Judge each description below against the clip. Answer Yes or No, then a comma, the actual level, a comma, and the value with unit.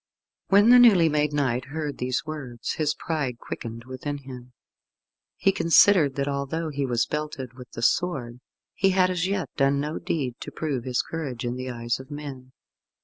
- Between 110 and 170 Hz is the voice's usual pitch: Yes, medium, 140 Hz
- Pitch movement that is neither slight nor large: Yes, average, 4.1 semitones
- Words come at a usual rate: Yes, average, 180 wpm